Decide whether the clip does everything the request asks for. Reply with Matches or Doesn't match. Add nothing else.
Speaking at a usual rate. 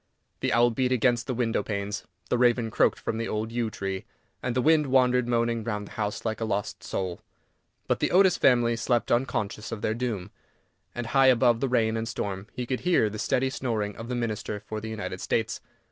Doesn't match